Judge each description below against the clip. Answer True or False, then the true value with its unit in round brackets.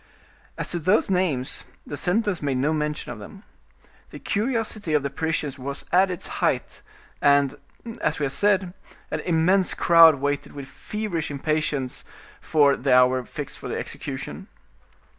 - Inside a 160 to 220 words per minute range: False (150 wpm)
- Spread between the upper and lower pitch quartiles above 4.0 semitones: True (4.8 semitones)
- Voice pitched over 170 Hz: False (155 Hz)